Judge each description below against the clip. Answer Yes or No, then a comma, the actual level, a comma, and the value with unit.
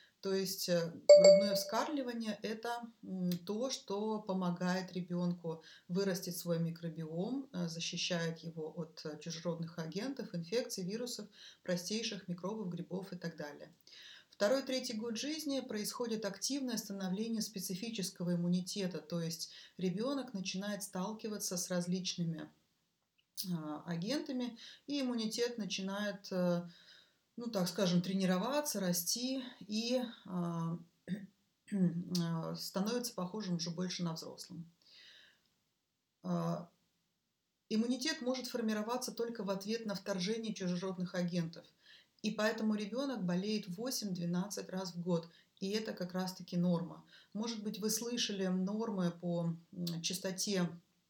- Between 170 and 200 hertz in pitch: Yes, high, 190 Hz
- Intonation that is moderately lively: Yes, average, 3.9 semitones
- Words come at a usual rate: No, slow, 105 wpm